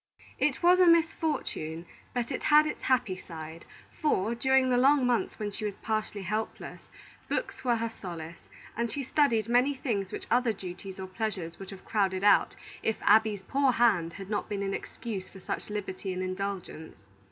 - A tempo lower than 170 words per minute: No, average, 180 wpm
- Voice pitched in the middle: No, high, 215 Hz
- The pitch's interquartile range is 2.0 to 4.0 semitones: No, average, 4.8 semitones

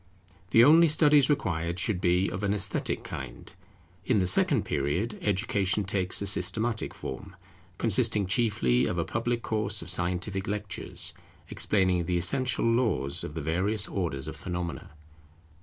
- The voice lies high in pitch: No, low, 100 Hz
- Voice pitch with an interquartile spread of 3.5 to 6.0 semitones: Yes, average, 4.3 semitones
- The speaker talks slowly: No, average, 145 wpm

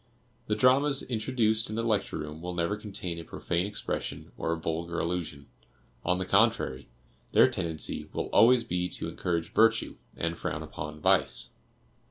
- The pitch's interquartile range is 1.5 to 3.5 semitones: No, average, 4.9 semitones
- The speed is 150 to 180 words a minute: Yes, average, 160 wpm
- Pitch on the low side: Yes, very low, 90 Hz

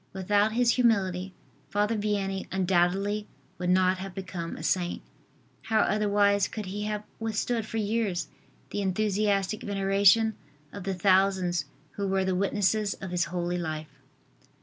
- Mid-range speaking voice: No, high, 195 Hz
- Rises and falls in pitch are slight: Yes, narrow, 2.2 semitones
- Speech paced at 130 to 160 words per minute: Yes, average, 140 wpm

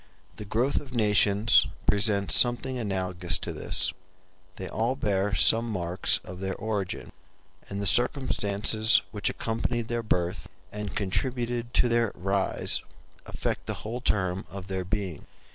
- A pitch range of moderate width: Yes, average, 3.5 semitones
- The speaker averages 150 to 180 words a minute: No, average, 140 wpm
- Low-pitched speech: Yes, low, 105 Hz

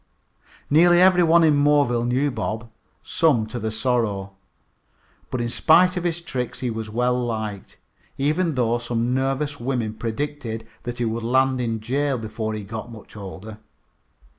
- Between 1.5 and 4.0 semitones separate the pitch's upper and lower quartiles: No, average, 4.4 semitones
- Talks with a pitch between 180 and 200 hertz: No, low, 120 Hz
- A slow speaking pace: No, average, 165 wpm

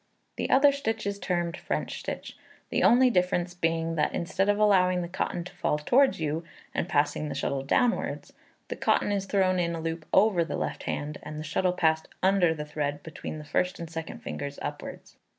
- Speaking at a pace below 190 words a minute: No, average, 200 wpm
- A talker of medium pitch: Yes, medium, 170 Hz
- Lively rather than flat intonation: No, average, 3.8 semitones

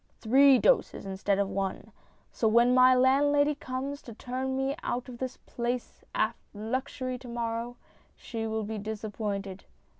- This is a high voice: Yes, high, 240 Hz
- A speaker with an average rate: Yes, average, 150 wpm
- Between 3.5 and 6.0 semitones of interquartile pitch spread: No, average, 3.1 semitones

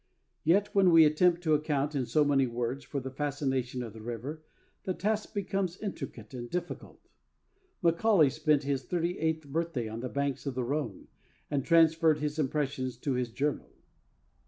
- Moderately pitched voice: Yes, medium, 145 Hz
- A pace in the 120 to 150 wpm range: No, average, 170 wpm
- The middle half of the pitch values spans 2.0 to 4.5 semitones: Yes, average, 4.2 semitones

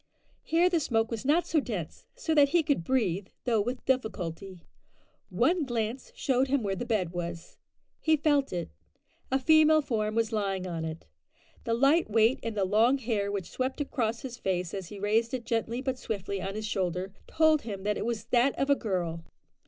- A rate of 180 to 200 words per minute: Yes, average, 195 wpm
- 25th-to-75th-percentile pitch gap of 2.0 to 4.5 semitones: No, wide, 5.5 semitones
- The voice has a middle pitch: No, high, 225 Hz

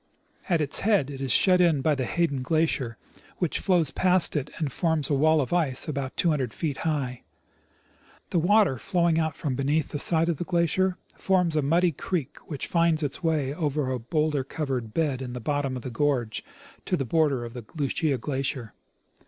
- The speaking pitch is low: No, medium, 150 Hz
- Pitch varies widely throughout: No, average, 3.9 semitones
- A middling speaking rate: Yes, average, 195 wpm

